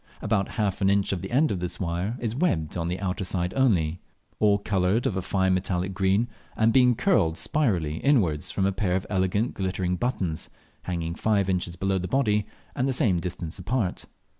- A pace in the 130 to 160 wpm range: No, average, 195 wpm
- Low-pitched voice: Yes, very low, 95 Hz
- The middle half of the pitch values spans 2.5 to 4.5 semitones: Yes, average, 3.3 semitones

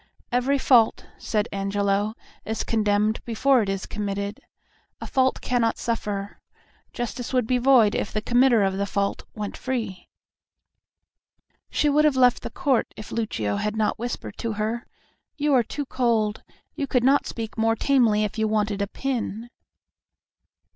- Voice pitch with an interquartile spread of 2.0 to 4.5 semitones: Yes, average, 3.2 semitones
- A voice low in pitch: No, high, 225 Hz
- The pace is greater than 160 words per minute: No, average, 155 wpm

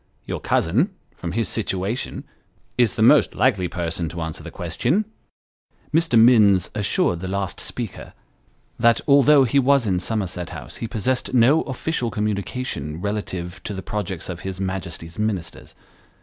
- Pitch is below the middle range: Yes, low, 105 Hz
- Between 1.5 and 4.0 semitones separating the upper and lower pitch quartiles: No, average, 5.3 semitones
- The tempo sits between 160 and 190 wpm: No, average, 150 wpm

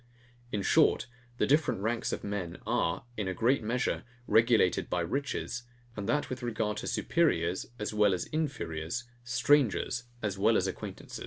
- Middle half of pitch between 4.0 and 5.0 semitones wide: Yes, average, 4.3 semitones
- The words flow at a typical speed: Yes, average, 160 wpm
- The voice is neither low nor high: No, low, 110 Hz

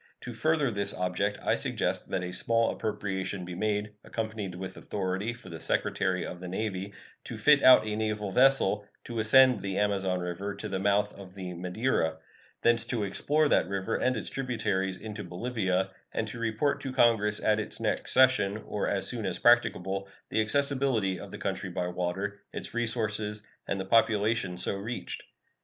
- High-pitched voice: No, low, 105 Hz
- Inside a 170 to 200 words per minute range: Yes, average, 180 wpm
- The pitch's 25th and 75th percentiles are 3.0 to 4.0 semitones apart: Yes, average, 3.3 semitones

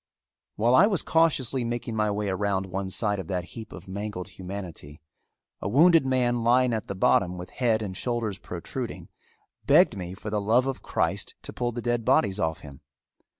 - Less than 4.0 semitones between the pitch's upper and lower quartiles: No, average, 4.3 semitones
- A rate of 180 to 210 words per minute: Yes, average, 190 wpm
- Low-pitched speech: Yes, low, 105 Hz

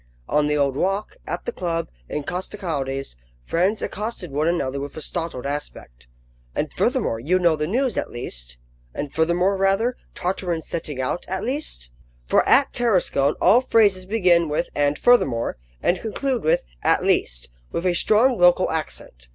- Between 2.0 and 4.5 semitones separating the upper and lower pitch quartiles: No, wide, 5.4 semitones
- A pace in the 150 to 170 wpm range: Yes, average, 160 wpm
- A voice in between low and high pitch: Yes, medium, 170 Hz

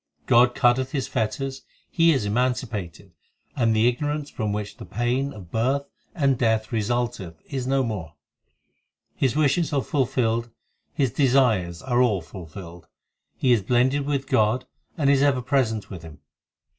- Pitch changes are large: No, average, 4.2 semitones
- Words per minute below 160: Yes, average, 150 wpm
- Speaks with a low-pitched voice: Yes, low, 120 Hz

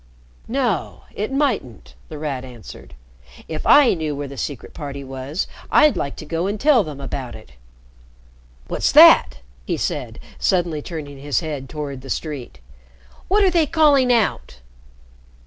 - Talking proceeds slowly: No, average, 150 wpm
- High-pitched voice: No, medium, 155 Hz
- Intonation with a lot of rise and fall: Yes, wide, 8.9 semitones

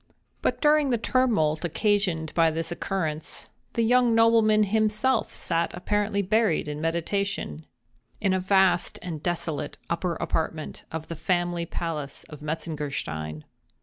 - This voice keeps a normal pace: No, slow, 130 wpm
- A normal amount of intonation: Yes, average, 5.0 semitones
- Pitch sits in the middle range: Yes, medium, 175 Hz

